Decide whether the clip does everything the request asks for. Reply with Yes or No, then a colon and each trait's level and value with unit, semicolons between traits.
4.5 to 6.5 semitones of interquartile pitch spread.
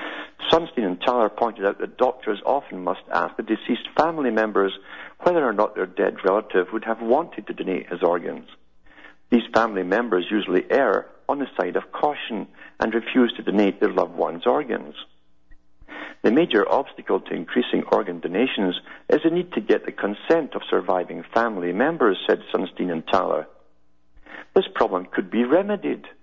Yes: average, 4.8 semitones